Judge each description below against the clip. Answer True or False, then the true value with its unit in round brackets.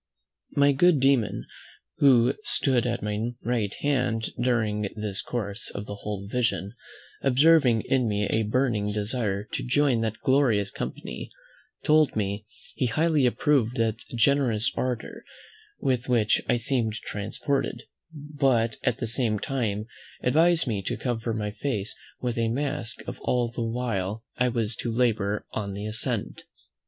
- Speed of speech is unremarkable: True (145 wpm)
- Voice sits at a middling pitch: False (115 Hz)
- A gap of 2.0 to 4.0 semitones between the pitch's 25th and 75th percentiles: True (3.6 semitones)